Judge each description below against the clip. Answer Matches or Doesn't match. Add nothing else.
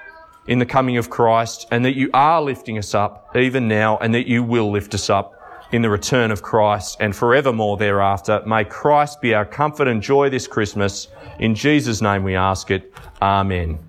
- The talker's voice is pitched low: Matches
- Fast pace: Doesn't match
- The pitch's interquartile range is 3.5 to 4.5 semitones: Matches